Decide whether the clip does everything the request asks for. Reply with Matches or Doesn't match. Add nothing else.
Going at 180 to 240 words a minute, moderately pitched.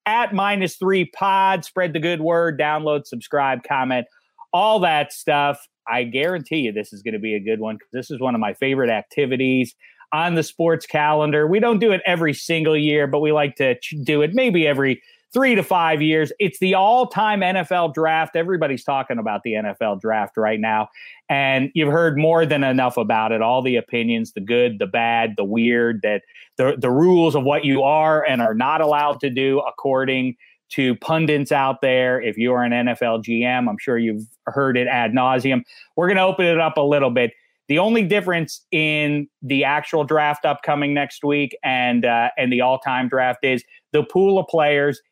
Matches